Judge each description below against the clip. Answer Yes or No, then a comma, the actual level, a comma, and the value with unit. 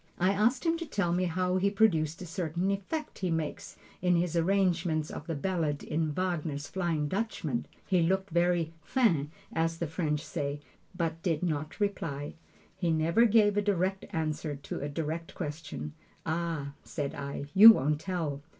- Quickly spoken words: No, average, 170 wpm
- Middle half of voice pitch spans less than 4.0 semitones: Yes, average, 3.6 semitones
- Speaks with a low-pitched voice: No, medium, 170 Hz